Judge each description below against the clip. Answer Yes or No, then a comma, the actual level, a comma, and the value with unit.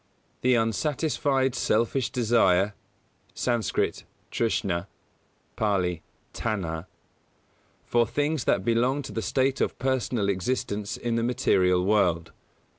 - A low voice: Yes, low, 115 Hz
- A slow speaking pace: Yes, slow, 105 wpm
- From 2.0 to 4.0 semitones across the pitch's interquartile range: No, average, 4.6 semitones